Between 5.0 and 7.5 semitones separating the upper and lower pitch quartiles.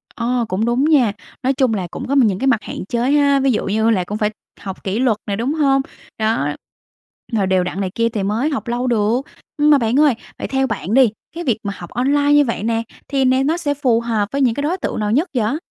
No: average, 4.3 semitones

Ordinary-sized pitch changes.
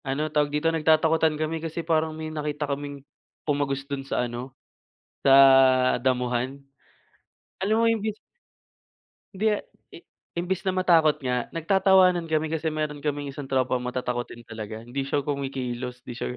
Yes: average, 3.7 semitones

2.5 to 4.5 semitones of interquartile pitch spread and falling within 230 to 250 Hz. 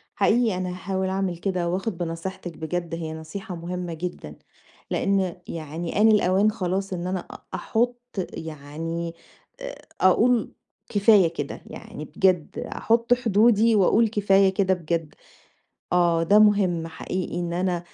No: average, 3.2 semitones; medium, 185 Hz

